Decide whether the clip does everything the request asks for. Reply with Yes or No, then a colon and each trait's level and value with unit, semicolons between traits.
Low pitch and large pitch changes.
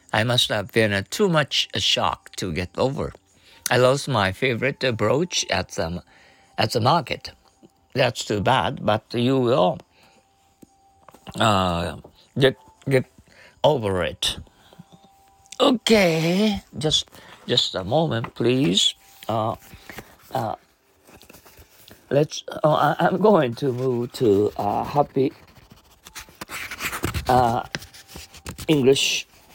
Yes: low, 125 Hz; wide, 7.1 semitones